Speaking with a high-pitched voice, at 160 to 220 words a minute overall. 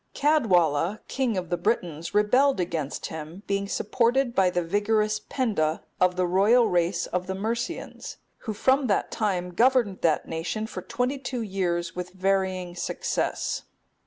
No: high, 195 Hz; average, 150 wpm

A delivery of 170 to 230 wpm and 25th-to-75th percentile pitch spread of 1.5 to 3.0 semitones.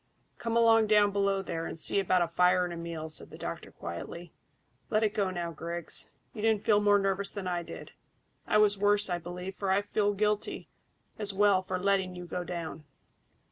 Yes: fast, 205 wpm; average, 2.7 semitones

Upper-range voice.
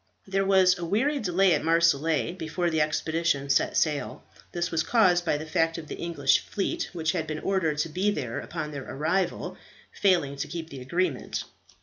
No: medium, 165 Hz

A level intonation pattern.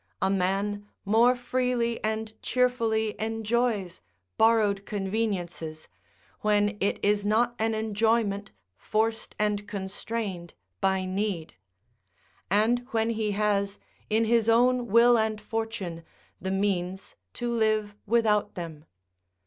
Yes: narrow, 2.3 semitones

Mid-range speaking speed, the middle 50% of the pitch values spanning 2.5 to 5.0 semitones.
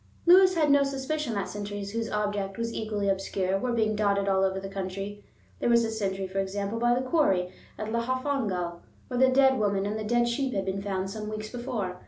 No: fast, 215 wpm; average, 3.6 semitones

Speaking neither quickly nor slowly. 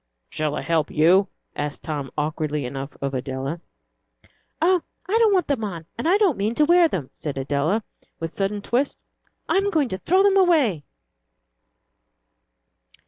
Yes: average, 160 wpm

